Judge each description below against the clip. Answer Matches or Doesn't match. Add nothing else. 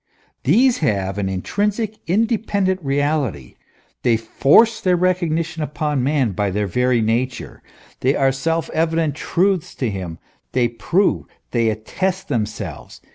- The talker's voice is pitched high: Doesn't match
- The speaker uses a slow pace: Matches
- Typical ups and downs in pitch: Doesn't match